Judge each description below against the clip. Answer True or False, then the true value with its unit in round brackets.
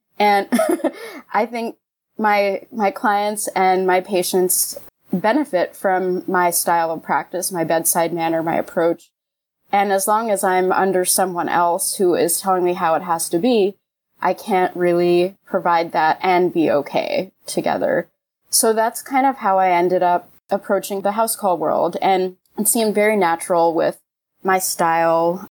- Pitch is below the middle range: False (185 Hz)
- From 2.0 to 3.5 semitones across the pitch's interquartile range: True (2.9 semitones)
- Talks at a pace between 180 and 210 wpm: False (155 wpm)